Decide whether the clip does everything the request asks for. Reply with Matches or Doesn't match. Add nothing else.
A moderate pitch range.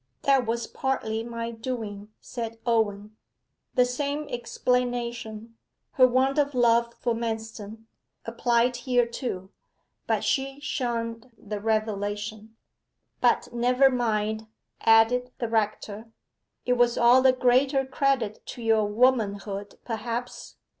Doesn't match